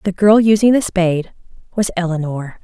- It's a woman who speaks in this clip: Yes, female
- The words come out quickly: No, average, 160 wpm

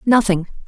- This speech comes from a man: No, female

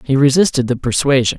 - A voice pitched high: No, low, 135 Hz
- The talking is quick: No, average, 175 wpm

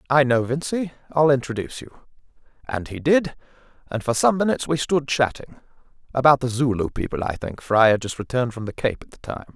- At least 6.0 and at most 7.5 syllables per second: Yes, 6.1 syllables/s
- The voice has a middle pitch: No, low, 130 Hz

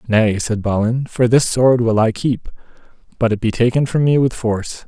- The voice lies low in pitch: Yes, low, 115 Hz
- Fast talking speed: Yes, fast, 210 wpm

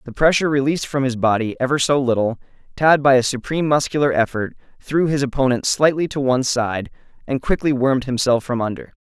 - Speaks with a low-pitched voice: Yes, low, 130 Hz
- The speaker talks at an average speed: Yes, average, 185 wpm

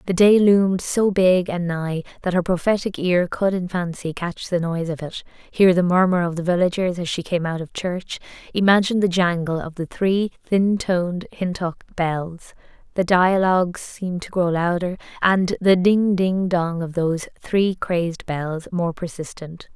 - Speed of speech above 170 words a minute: Yes, average, 180 wpm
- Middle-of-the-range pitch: Yes, medium, 180 Hz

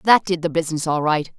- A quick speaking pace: Yes, fast, 260 wpm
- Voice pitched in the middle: Yes, medium, 165 Hz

